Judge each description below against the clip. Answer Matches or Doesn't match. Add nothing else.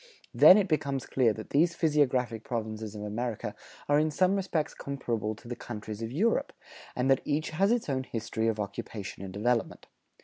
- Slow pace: Doesn't match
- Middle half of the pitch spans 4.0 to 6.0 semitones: Matches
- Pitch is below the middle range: Matches